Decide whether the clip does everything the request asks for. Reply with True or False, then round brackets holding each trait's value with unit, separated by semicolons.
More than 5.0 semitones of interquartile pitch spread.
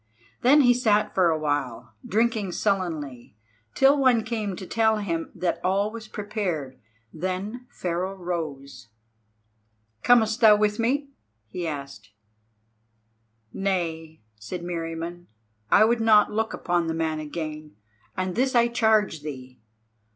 True (5.4 semitones)